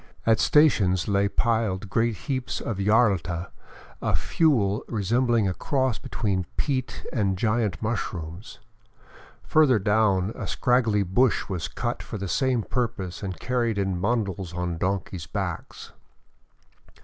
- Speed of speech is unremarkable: No, slow, 130 wpm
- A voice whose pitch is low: Yes, low, 105 Hz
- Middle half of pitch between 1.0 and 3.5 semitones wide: No, average, 4.1 semitones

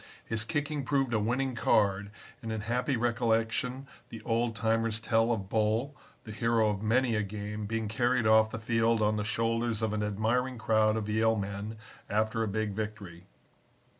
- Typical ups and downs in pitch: No, narrow, 1.6 semitones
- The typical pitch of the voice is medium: No, low, 110 Hz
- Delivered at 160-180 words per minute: Yes, average, 175 wpm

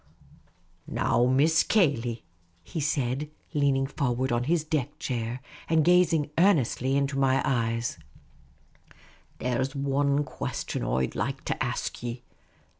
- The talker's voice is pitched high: No, low, 135 Hz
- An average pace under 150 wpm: Yes, average, 140 wpm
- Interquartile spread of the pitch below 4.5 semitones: Yes, average, 3.4 semitones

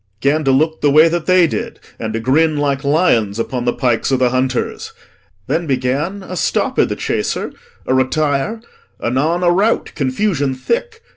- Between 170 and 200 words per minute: Yes, average, 175 wpm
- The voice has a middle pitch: Yes, medium, 145 Hz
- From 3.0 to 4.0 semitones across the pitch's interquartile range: No, average, 4.8 semitones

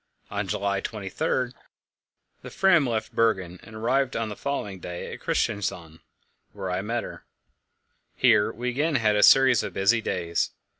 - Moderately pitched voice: No, low, 110 Hz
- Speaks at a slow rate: No, average, 155 wpm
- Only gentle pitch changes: No, average, 4.4 semitones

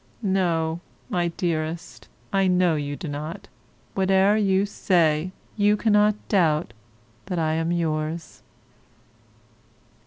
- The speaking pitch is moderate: Yes, medium, 175 Hz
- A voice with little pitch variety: No, average, 3.4 semitones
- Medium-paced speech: No, slow, 105 wpm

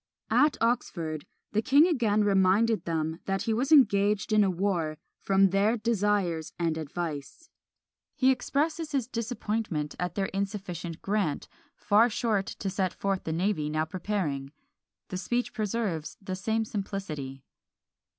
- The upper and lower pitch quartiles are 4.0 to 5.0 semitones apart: Yes, average, 4.7 semitones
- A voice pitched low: No, high, 195 Hz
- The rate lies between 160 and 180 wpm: No, average, 140 wpm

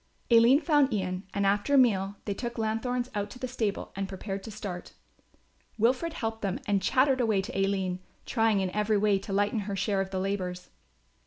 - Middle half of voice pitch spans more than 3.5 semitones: No, average, 3.2 semitones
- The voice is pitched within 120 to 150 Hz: No, high, 205 Hz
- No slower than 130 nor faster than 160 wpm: No, average, 195 wpm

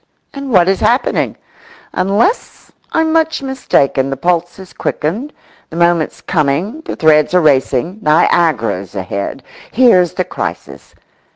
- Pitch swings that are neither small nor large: No, wide, 7.4 semitones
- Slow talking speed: Yes, slow, 120 wpm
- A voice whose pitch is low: No, medium, 175 Hz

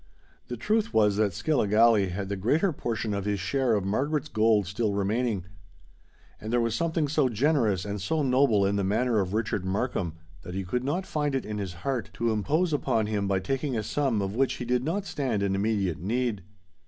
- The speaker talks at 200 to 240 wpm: Yes, fast, 205 wpm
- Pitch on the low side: Yes, low, 110 Hz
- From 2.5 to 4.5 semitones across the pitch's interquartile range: No, average, 5.1 semitones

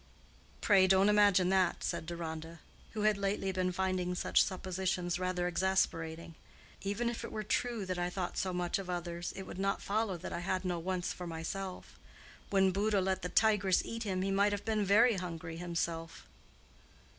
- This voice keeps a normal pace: Yes, average, 180 wpm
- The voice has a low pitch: No, medium, 185 Hz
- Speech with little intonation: Yes, narrow, 2.0 semitones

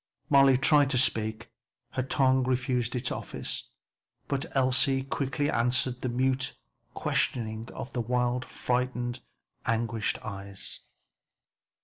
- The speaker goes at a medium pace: No, slow, 110 wpm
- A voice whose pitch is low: Yes, low, 125 Hz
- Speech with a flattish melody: Yes, narrow, 2.0 semitones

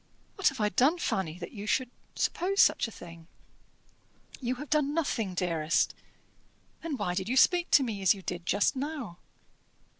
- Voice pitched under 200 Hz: No, high, 225 Hz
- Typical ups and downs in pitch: No, wide, 8.1 semitones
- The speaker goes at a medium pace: Yes, average, 160 wpm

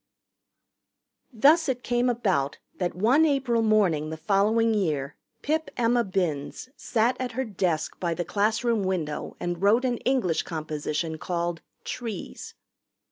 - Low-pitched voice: No, high, 205 Hz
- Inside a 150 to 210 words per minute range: No, slow, 135 wpm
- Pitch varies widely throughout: Yes, wide, 6.2 semitones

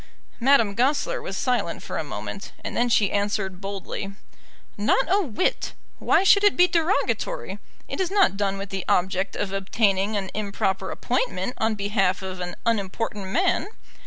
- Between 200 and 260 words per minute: No, average, 160 wpm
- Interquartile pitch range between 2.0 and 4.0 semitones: No, average, 4.6 semitones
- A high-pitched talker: Yes, high, 205 Hz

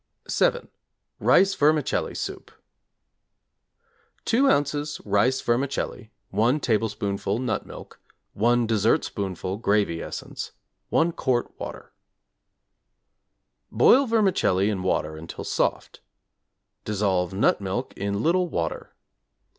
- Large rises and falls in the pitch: Yes, wide, 6.8 semitones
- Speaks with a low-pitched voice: Yes, low, 110 Hz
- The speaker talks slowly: Yes, slow, 95 wpm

